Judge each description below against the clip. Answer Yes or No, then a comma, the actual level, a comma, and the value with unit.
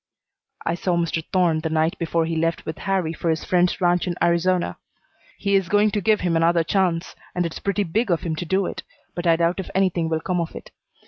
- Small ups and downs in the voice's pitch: Yes, narrow, 2.1 semitones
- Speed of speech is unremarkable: No, fast, 235 wpm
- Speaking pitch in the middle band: Yes, medium, 175 Hz